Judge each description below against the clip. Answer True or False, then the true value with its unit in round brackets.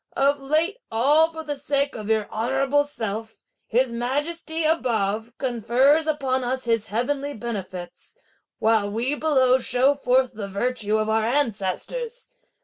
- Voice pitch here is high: True (255 Hz)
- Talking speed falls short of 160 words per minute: True (140 wpm)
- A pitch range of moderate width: True (4.6 semitones)